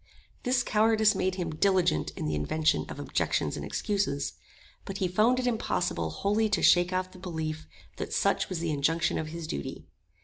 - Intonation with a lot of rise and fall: No, average, 4.7 semitones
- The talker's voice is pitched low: No, medium, 180 Hz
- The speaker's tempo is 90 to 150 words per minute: No, average, 180 wpm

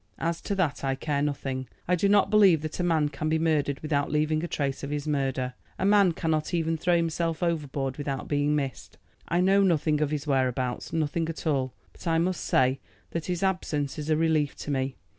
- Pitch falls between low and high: Yes, medium, 155 Hz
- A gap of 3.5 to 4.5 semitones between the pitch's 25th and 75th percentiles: No, average, 3.0 semitones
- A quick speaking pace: Yes, fast, 215 wpm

